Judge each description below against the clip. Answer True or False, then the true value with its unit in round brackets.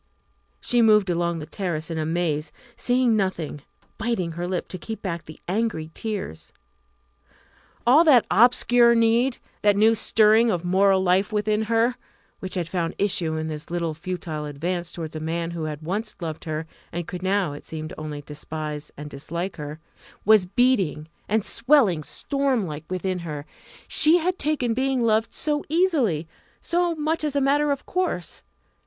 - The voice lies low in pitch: False (185 Hz)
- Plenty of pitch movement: True (6.5 semitones)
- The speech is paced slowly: False (165 wpm)